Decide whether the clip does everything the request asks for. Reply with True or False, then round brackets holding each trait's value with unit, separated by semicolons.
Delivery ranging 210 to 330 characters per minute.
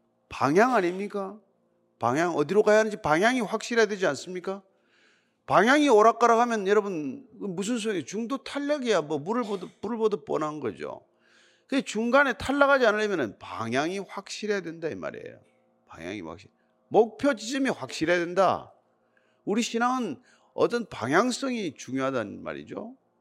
True (325 characters per minute)